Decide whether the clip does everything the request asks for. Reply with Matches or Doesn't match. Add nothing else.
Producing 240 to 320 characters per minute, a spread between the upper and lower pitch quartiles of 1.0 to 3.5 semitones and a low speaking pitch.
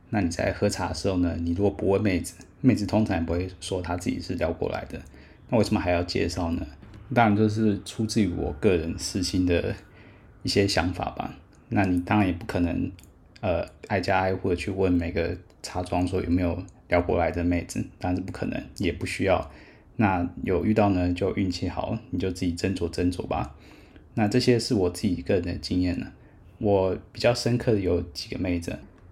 Matches